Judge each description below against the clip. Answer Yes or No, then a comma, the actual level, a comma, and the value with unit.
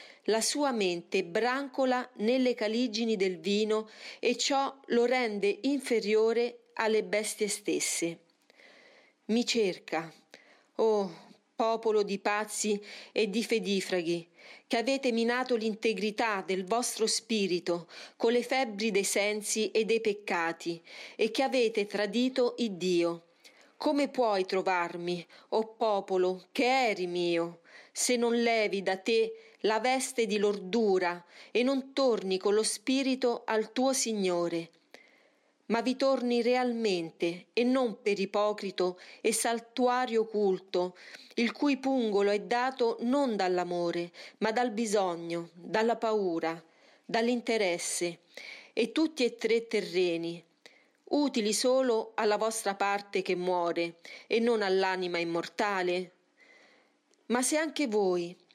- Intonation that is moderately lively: Yes, average, 4.4 semitones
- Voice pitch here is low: No, high, 215 Hz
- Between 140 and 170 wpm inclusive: No, average, 120 wpm